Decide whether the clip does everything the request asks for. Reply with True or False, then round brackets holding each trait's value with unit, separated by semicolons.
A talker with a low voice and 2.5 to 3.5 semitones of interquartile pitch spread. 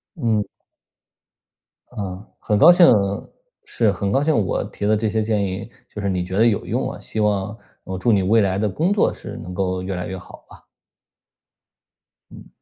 True (105 Hz; 2.9 semitones)